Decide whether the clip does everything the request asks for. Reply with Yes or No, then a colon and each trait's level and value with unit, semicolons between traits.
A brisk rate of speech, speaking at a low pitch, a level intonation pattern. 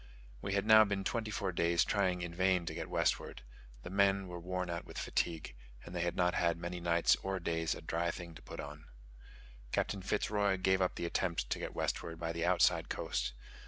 Yes: fast, 220 wpm; very low, 90 Hz; narrow, 2.3 semitones